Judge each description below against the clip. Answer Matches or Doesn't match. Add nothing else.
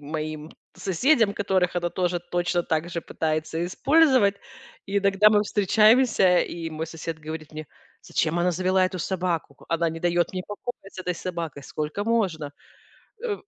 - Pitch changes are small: Doesn't match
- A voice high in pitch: Doesn't match